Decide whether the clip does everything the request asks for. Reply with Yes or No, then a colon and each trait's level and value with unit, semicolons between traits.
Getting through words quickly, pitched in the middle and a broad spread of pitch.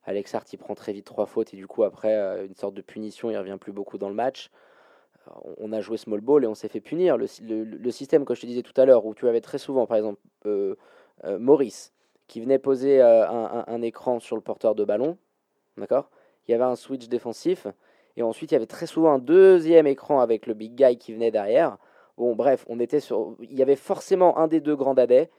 No: fast, 250 wpm; low, 125 Hz; wide, 6.3 semitones